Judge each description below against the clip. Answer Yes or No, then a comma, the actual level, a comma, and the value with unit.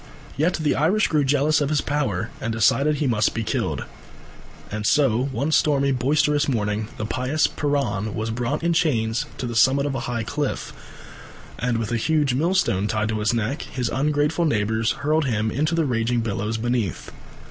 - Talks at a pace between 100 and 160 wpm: No, average, 180 wpm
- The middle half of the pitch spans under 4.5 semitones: No, average, 4.8 semitones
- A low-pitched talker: Yes, low, 130 Hz